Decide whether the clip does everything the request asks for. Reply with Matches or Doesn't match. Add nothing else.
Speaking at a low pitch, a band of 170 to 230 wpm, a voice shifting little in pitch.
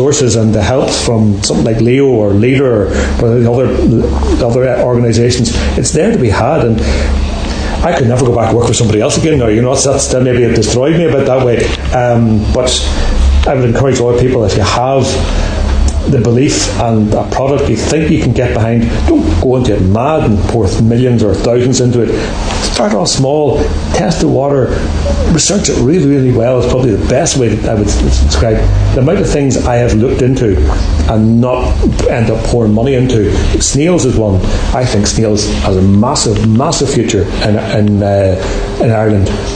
Doesn't match